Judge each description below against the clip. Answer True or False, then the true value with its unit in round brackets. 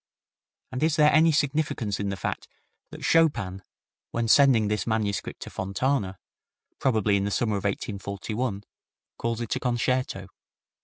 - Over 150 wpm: False (145 wpm)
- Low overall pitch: True (115 Hz)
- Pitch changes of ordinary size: True (4.9 semitones)